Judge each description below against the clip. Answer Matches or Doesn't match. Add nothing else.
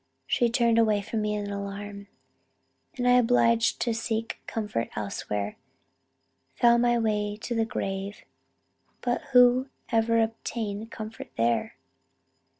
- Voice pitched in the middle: Doesn't match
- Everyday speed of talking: Doesn't match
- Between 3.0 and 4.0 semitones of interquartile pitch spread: Doesn't match